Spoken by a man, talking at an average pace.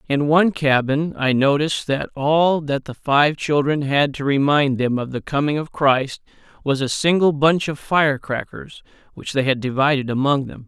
Yes: male; average, 180 wpm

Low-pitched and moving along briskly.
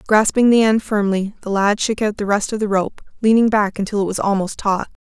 No: high, 205 Hz; fast, 240 wpm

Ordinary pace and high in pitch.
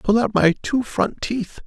No: fast, 215 wpm; high, 195 Hz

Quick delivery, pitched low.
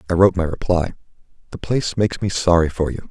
Yes: fast, 210 wpm; very low, 90 Hz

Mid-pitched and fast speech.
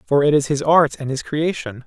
Yes: medium, 145 Hz; fast, 260 wpm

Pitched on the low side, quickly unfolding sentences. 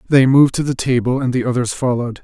Yes: low, 125 Hz; fast, 240 wpm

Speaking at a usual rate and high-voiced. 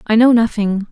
Yes: average, 195 wpm; high, 220 Hz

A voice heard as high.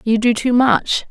Yes: high, 235 Hz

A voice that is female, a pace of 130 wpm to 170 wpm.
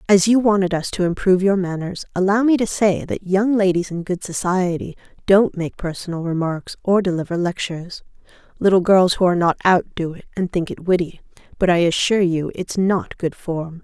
No: female; average, 195 wpm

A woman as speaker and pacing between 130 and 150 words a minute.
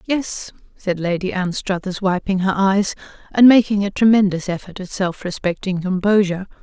Yes: female; average, 145 wpm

